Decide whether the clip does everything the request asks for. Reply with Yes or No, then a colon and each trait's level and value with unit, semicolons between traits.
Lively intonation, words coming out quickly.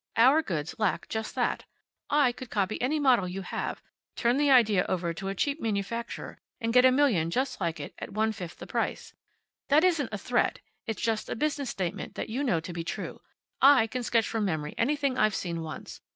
Yes: wide, 5.8 semitones; fast, 210 wpm